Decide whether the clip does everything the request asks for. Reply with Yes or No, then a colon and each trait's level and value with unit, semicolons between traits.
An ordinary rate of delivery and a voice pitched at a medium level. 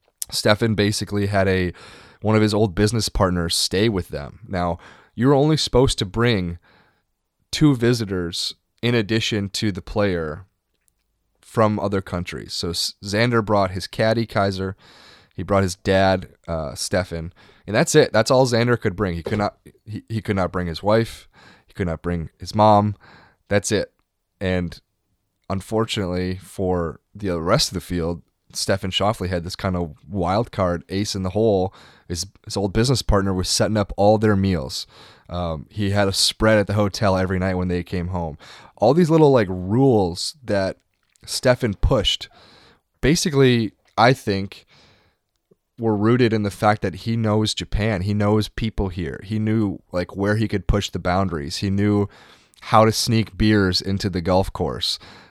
No: average, 170 wpm; low, 100 Hz